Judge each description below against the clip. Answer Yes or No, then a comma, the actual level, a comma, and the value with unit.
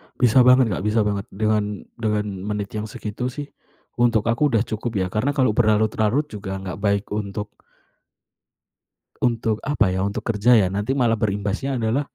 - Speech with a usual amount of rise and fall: No, narrow, 2.3 semitones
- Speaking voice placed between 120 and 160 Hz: No, low, 110 Hz